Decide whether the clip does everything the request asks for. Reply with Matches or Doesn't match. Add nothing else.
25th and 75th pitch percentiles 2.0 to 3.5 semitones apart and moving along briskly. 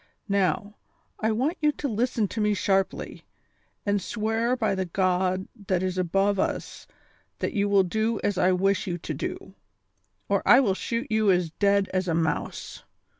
Doesn't match